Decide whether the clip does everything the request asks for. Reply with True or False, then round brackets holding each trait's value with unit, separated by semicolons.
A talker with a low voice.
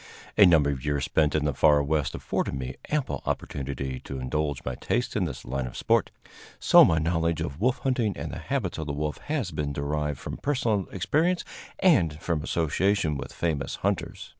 True (75 Hz)